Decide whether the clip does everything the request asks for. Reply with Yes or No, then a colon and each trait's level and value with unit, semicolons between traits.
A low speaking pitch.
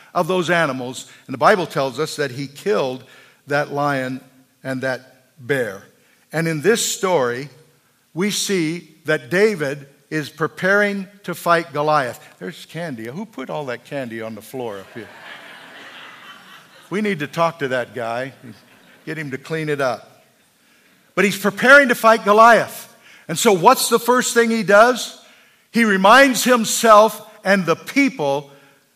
No: medium, 160 Hz